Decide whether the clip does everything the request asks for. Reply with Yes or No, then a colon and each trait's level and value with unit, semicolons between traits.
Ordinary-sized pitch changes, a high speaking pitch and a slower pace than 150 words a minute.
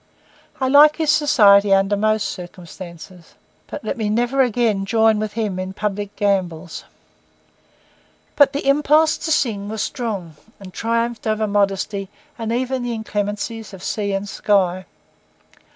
Yes: average, 3.3 semitones; high, 210 Hz; average, 140 wpm